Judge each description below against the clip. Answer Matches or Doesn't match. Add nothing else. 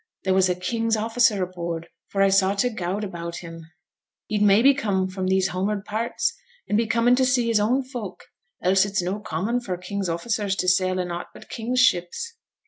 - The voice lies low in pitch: Doesn't match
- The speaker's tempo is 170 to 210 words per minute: Matches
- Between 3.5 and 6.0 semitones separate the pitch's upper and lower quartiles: Matches